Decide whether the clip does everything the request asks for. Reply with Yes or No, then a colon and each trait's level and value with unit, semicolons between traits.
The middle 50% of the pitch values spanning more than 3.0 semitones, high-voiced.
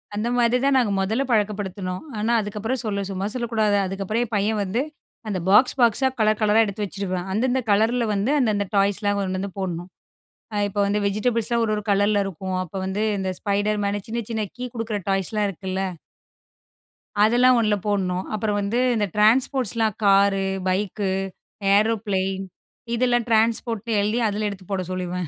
No: narrow, 2.5 semitones; high, 210 Hz